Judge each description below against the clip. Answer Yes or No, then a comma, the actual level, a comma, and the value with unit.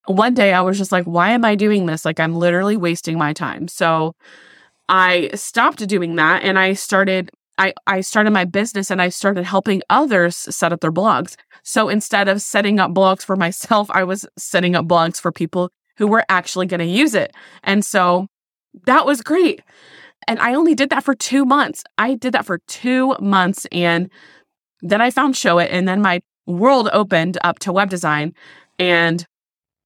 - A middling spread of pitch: Yes, average, 3.5 semitones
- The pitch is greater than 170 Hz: Yes, high, 190 Hz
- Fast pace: No, average, 195 wpm